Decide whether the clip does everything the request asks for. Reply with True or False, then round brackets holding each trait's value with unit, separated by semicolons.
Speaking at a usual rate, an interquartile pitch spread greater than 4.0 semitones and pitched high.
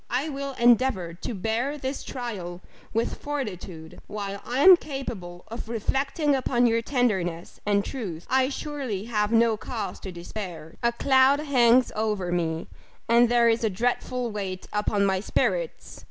True (155 wpm; 5.0 semitones; 230 Hz)